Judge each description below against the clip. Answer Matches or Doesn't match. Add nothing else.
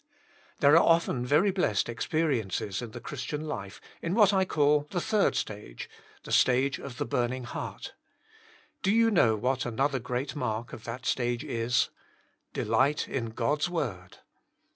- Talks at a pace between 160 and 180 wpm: Matches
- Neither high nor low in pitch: Doesn't match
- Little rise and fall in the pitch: Doesn't match